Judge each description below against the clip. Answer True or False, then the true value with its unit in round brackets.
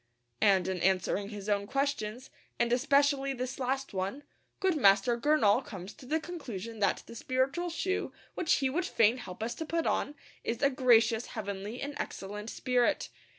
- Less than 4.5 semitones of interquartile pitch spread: False (5.3 semitones)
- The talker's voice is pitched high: True (245 Hz)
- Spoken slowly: False (170 wpm)